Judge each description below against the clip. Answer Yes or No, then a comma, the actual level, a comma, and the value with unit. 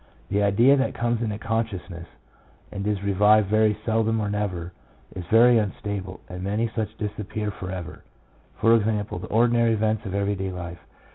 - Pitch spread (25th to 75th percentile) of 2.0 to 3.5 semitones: Yes, narrow, 2.6 semitones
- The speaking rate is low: No, average, 170 wpm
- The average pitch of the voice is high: No, low, 105 Hz